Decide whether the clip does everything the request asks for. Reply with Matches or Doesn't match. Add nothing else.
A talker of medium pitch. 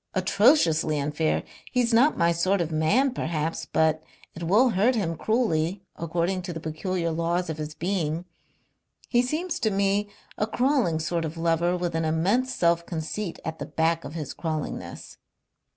Matches